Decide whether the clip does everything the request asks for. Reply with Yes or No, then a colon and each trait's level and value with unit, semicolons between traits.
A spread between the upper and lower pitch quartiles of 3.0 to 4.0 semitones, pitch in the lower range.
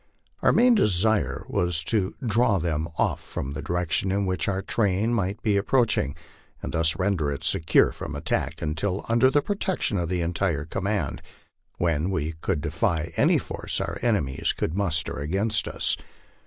No: average, 4.7 semitones; very low, 95 Hz